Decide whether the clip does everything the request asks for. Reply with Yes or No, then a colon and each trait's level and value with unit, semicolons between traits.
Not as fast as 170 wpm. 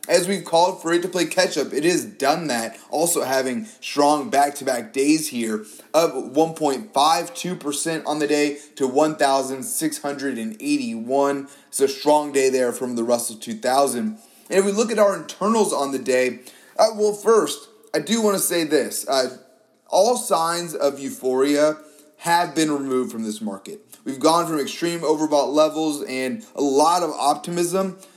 Yes: average, 160 wpm